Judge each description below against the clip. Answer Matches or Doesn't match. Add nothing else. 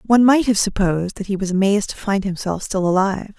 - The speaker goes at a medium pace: Doesn't match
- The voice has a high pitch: Matches